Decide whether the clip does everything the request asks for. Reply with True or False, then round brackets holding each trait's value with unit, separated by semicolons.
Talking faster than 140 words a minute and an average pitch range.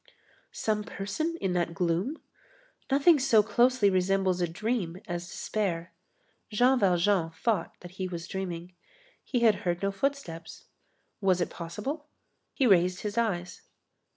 False (135 wpm; 4.7 semitones)